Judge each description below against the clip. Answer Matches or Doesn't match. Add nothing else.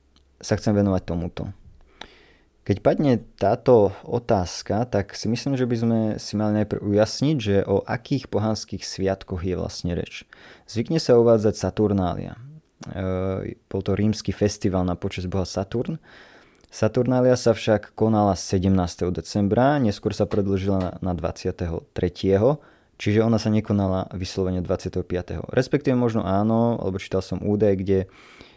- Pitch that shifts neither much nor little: Matches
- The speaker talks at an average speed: Matches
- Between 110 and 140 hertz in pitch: Doesn't match